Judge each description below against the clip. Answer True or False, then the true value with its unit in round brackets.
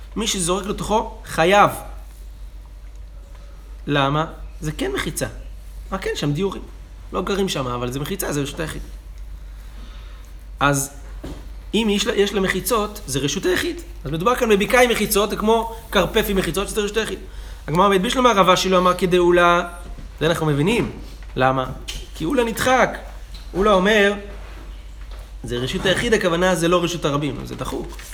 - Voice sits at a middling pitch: True (175 Hz)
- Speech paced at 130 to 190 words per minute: True (150 wpm)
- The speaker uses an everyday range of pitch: False (8.7 semitones)